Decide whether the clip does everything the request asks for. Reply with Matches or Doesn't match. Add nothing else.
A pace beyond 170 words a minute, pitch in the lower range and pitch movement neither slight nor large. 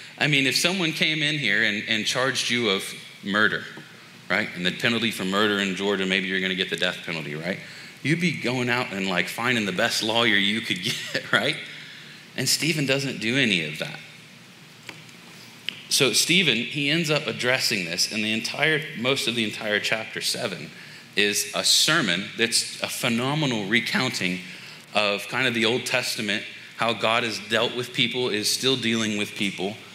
Matches